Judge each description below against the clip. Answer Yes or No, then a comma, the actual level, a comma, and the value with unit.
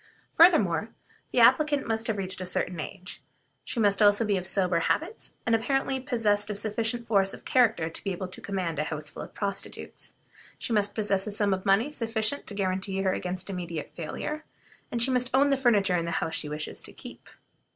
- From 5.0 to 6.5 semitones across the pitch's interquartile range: No, average, 3.8 semitones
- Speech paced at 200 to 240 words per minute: Yes, fast, 205 wpm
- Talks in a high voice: Yes, high, 205 Hz